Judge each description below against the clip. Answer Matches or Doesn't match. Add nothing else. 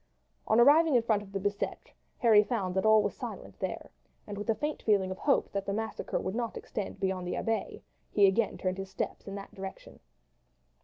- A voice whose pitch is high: Matches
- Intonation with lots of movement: Doesn't match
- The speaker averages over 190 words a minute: Matches